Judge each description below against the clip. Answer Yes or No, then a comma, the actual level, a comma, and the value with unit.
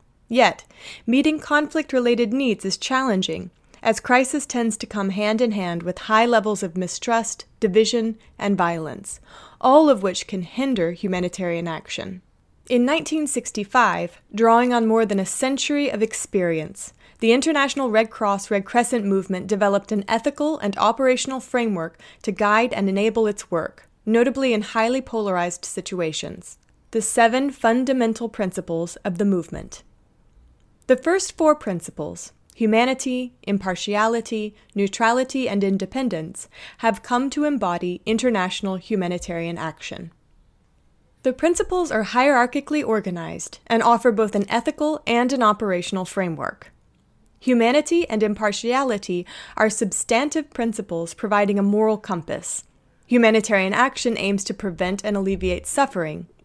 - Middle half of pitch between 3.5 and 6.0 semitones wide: Yes, average, 4.3 semitones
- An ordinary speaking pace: No, slow, 125 wpm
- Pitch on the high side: Yes, high, 220 Hz